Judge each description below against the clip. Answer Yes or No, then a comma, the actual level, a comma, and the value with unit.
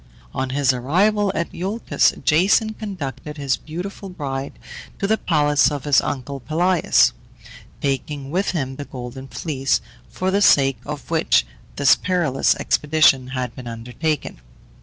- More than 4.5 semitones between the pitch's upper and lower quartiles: Yes, average, 5.1 semitones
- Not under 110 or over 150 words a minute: Yes, average, 140 wpm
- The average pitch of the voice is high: No, medium, 145 Hz